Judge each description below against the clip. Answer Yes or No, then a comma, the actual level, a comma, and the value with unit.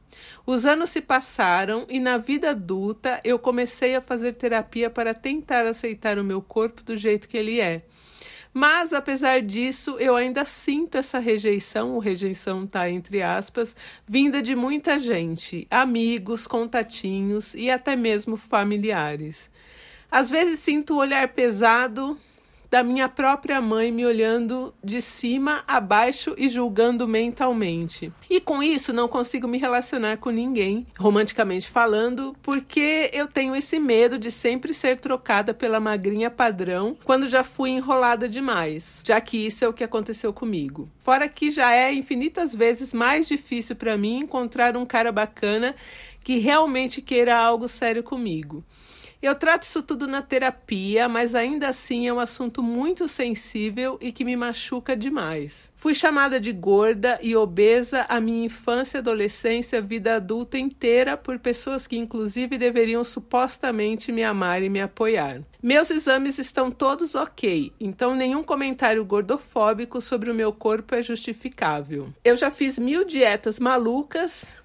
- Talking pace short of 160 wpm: Yes, average, 150 wpm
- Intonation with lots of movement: No, average, 3.0 semitones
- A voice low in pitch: No, high, 245 Hz